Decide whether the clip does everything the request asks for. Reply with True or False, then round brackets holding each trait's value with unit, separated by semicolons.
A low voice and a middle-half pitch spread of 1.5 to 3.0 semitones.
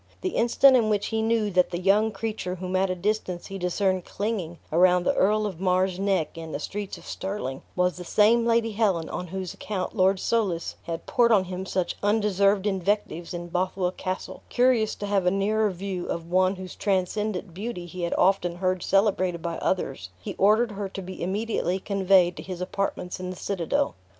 False (190 Hz; 2.5 semitones)